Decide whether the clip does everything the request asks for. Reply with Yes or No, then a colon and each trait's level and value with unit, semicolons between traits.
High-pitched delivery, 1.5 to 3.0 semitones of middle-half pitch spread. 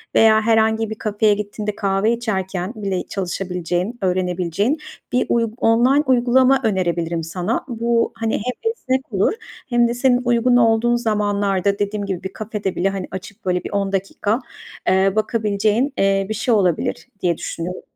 No: high, 210 Hz; average, 3.5 semitones